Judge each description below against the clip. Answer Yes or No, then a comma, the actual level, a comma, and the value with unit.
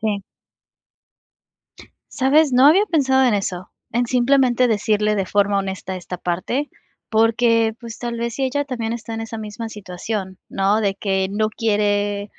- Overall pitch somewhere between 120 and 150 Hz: No, high, 220 Hz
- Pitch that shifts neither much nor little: Yes, average, 3.3 semitones